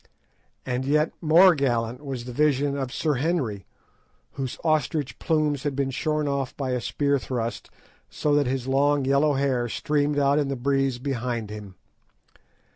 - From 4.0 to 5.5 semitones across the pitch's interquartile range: No, narrow, 2.6 semitones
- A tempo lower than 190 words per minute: Yes, average, 160 wpm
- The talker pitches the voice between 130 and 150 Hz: Yes, medium, 140 Hz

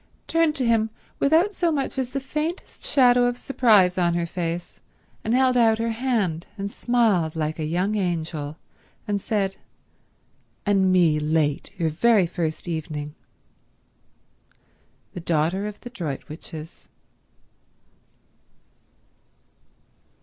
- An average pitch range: No, wide, 6.9 semitones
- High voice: Yes, high, 195 Hz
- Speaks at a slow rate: Yes, slow, 120 wpm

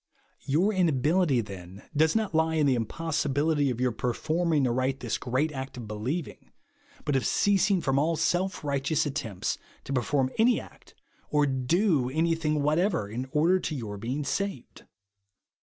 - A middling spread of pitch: Yes, average, 4.3 semitones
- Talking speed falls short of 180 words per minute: Yes, average, 155 wpm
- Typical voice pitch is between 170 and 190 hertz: No, medium, 145 Hz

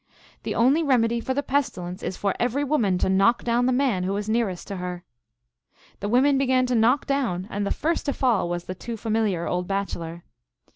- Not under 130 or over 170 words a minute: No, fast, 205 wpm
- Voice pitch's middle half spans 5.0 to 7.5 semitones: Yes, wide, 5.6 semitones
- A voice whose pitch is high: Yes, high, 225 Hz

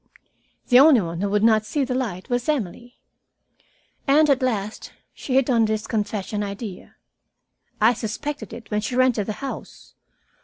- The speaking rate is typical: Yes, average, 160 wpm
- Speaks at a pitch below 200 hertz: No, high, 225 Hz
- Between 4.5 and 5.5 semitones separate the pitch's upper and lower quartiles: No, average, 3.6 semitones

